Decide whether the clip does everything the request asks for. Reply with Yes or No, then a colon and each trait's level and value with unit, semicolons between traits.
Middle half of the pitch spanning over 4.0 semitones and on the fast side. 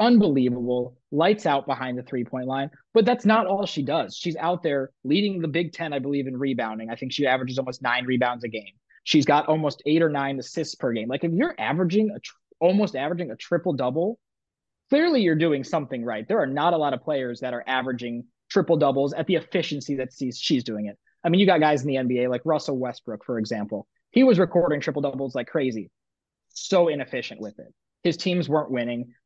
Yes: average, 5.2 semitones; fast, 215 wpm